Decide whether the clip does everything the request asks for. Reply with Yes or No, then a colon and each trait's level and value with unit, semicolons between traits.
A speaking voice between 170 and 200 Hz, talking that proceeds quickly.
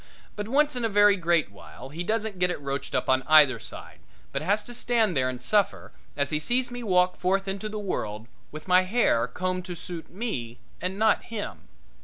Yes: medium, 185 Hz; fast, 210 wpm